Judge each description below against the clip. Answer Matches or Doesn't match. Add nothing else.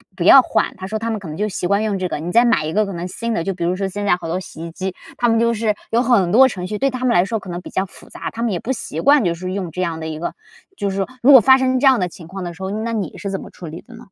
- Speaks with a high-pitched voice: Matches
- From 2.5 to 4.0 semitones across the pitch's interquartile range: Doesn't match